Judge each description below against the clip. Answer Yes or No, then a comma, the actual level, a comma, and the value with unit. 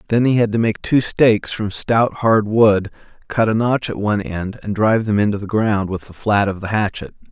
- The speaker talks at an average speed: No, fast, 240 wpm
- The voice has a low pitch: Yes, low, 105 Hz